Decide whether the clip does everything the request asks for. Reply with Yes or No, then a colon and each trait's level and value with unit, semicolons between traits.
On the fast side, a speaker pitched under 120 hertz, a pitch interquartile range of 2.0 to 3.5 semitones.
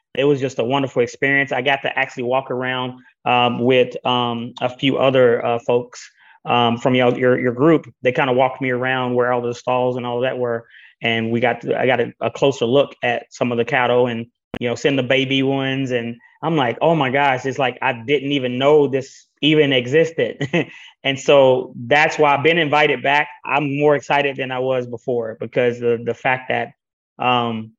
No: fast, 210 wpm; low, 130 Hz; narrow, 2.4 semitones